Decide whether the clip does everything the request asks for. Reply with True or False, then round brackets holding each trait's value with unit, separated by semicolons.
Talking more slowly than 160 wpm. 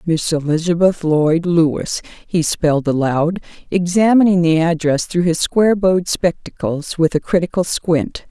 True (135 wpm)